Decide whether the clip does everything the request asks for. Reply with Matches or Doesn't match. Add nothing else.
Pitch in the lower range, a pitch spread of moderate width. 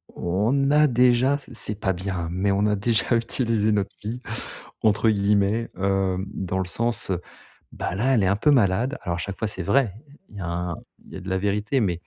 Matches